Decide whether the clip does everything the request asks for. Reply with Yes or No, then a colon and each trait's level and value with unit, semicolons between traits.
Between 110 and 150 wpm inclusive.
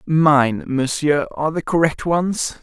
Yes: slow, 135 wpm